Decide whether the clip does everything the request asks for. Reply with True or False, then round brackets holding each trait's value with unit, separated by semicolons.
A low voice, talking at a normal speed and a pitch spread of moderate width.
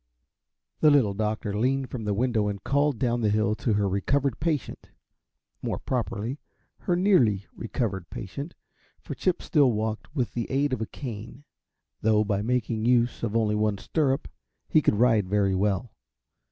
True (115 Hz; 165 wpm; 4.1 semitones)